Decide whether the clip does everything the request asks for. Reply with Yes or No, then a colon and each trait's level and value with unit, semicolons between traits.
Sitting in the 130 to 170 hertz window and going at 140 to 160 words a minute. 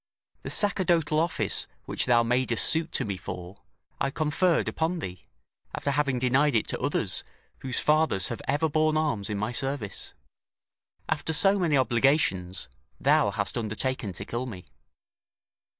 Yes: low, 135 Hz; average, 150 wpm